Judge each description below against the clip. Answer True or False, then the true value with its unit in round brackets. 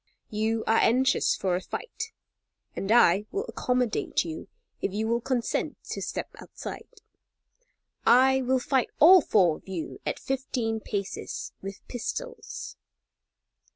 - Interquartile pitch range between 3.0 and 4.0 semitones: False (4.5 semitones)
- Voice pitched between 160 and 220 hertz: False (235 Hz)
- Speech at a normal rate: False (130 wpm)